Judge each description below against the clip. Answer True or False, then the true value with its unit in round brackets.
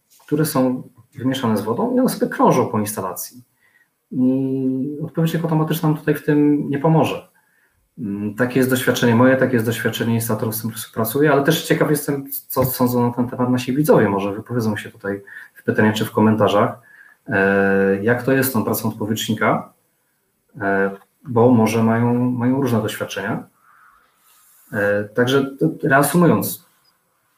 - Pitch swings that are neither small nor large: True (4.1 semitones)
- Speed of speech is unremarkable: True (145 wpm)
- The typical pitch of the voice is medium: False (125 Hz)